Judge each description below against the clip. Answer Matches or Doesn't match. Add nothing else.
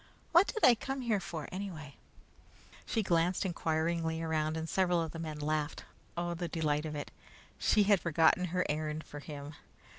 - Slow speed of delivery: Doesn't match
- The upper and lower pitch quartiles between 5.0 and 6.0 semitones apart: Doesn't match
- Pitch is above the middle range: Doesn't match